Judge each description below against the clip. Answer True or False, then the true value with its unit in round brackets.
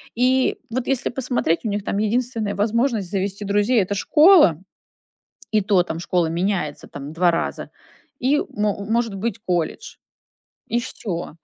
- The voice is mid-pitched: False (205 Hz)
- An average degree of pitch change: True (4.6 semitones)